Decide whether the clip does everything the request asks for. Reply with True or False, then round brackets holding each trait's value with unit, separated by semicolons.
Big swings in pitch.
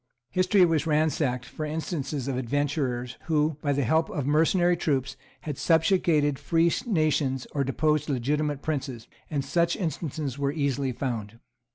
False (3.1 semitones)